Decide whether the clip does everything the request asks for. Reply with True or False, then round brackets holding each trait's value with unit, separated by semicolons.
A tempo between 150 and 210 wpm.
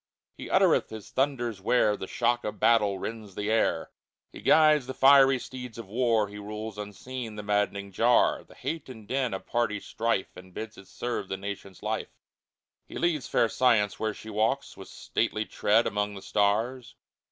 True (180 wpm)